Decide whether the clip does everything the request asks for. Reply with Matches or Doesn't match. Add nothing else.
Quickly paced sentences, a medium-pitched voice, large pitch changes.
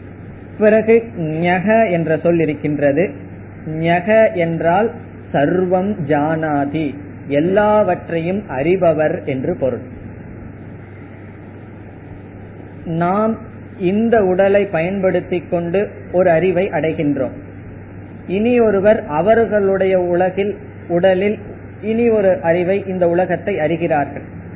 Doesn't match